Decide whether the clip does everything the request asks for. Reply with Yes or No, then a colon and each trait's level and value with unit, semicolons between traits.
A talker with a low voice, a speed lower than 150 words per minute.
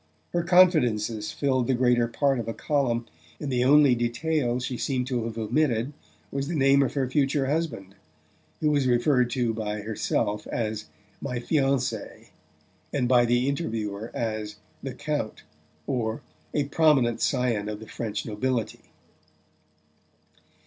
Yes: low, 125 Hz; average, 140 wpm